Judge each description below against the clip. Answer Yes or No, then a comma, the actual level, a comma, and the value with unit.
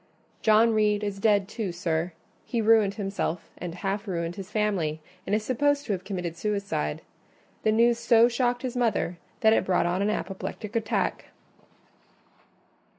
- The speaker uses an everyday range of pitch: Yes, average, 3.6 semitones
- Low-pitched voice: No, high, 210 Hz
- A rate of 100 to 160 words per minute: Yes, average, 155 wpm